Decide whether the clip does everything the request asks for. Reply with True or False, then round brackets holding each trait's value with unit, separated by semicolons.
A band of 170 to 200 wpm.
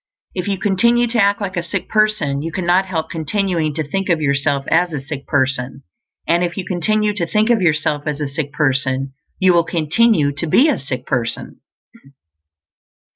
True (185 wpm)